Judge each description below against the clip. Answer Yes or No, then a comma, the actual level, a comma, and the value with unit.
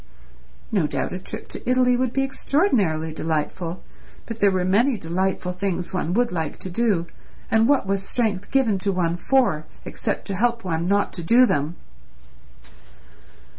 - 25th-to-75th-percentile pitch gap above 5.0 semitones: Yes, wide, 5.4 semitones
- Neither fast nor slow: Yes, average, 165 wpm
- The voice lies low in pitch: No, high, 195 Hz